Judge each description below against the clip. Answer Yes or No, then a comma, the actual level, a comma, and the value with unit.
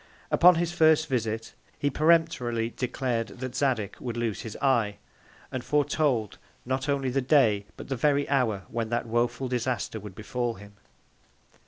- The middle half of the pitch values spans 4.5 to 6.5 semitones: No, average, 3.8 semitones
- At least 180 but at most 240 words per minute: No, average, 155 wpm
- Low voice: Yes, low, 125 Hz